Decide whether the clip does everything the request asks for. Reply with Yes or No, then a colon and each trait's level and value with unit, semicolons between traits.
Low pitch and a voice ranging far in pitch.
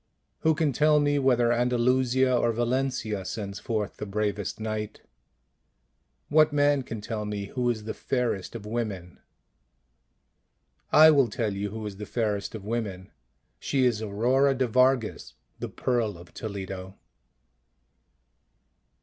No: low, 115 Hz; average, 3.8 semitones